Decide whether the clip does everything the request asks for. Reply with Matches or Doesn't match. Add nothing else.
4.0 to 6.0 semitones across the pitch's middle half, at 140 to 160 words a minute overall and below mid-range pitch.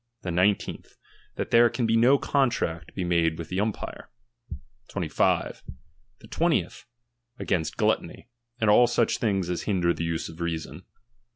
Matches